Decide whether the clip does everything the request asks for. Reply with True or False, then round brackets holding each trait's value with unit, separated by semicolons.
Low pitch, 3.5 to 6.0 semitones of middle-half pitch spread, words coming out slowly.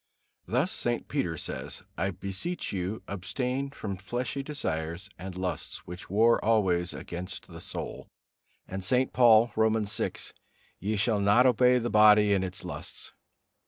False (105 Hz; 4.5 semitones; 145 wpm)